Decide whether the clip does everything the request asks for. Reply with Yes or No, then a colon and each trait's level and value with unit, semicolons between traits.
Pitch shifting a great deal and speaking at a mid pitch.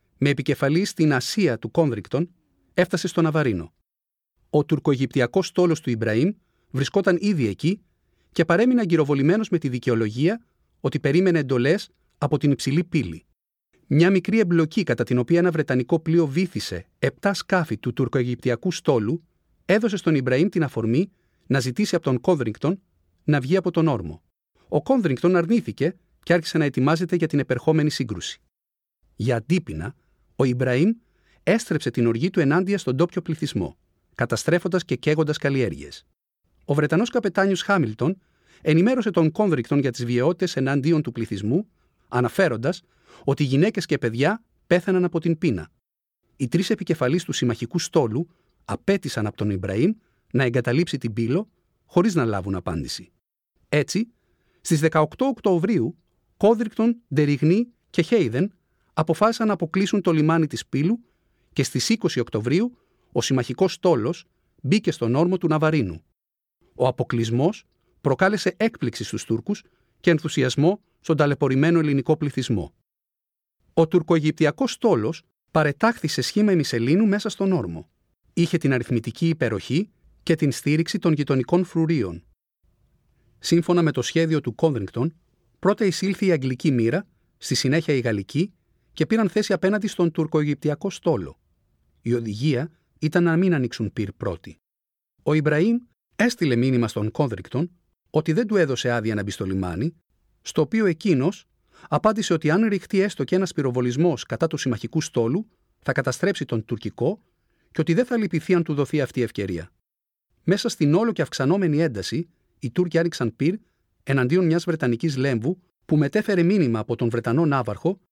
Yes: wide, 6.2 semitones; medium, 160 Hz